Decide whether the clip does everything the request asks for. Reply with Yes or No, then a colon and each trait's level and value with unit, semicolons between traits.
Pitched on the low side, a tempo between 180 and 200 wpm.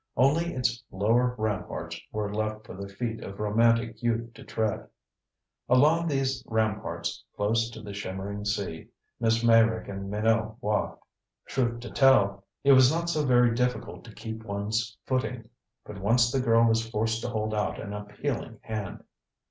No: low, 115 Hz; average, 160 wpm